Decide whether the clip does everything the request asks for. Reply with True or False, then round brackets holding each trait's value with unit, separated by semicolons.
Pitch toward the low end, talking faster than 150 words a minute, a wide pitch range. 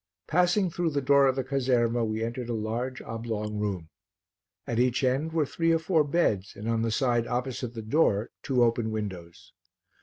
False (120 Hz; 185 wpm; 3.9 semitones)